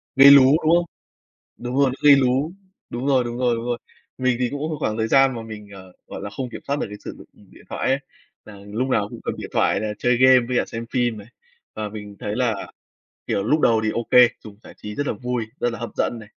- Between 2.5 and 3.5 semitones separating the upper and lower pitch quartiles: Yes, average, 3.2 semitones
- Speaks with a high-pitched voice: No, low, 120 Hz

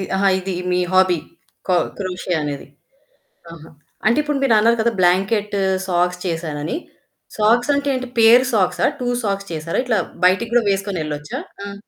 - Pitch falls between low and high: No, high, 195 Hz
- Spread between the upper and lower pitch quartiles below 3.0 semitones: No, average, 4.3 semitones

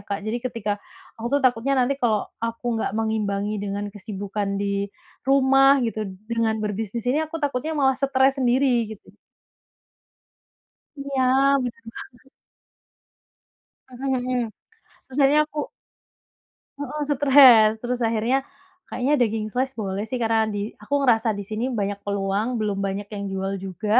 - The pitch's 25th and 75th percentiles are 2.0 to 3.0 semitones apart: No, average, 4.1 semitones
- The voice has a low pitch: No, high, 230 Hz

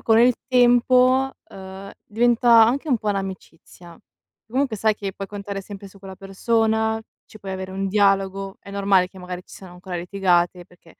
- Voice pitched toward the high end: Yes, high, 195 Hz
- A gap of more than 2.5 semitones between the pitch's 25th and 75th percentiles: Yes, average, 2.9 semitones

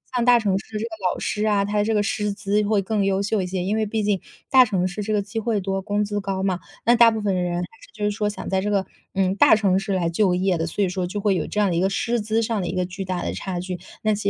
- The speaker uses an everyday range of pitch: No, narrow, 2.1 semitones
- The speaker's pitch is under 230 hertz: Yes, high, 200 Hz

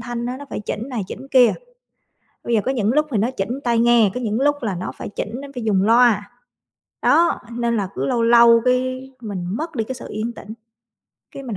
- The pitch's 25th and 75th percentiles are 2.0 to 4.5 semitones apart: Yes, average, 2.8 semitones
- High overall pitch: Yes, high, 235 Hz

